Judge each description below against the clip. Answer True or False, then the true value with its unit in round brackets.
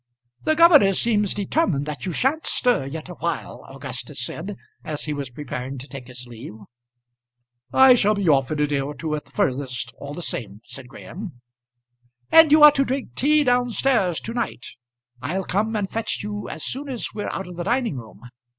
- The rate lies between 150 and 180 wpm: False (195 wpm)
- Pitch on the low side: False (180 Hz)